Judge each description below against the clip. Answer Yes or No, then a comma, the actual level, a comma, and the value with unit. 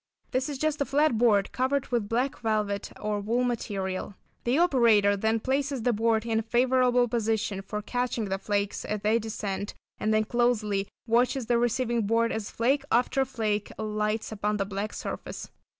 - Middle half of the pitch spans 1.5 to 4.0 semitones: Yes, average, 2.9 semitones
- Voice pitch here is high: Yes, high, 225 Hz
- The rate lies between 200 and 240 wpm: No, average, 175 wpm